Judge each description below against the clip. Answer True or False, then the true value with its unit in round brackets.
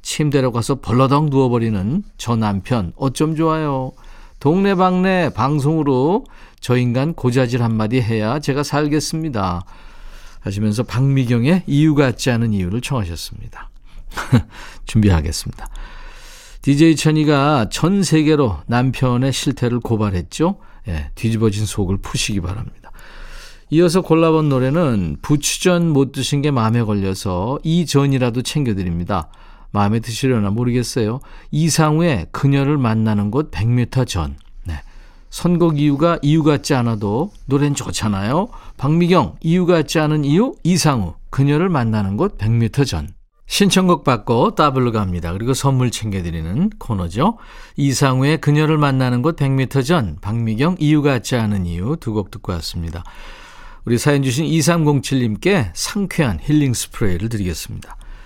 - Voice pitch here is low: True (130 Hz)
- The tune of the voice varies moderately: False (6.1 semitones)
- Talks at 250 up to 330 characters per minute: True (300 characters per minute)